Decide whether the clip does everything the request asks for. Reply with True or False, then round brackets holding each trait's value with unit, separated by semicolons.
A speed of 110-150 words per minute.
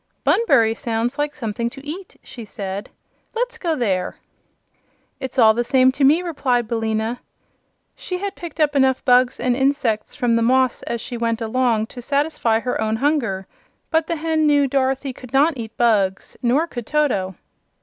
False (170 wpm)